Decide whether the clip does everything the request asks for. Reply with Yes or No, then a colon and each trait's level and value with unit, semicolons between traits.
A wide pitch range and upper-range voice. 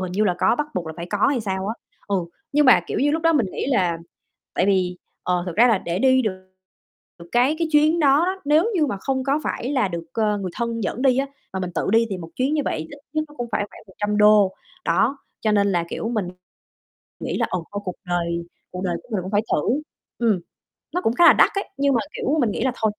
Yes: wide, 6.5 semitones; high, 220 Hz